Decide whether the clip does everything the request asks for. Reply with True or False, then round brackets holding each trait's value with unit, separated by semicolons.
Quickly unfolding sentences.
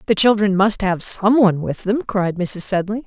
False (195 wpm)